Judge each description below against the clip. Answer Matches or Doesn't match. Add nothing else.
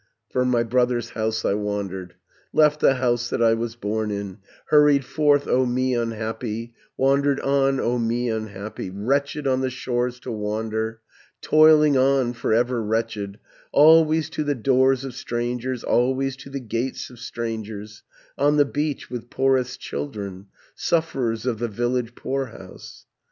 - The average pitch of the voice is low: Matches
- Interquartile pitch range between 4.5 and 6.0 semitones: Doesn't match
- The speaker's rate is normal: Matches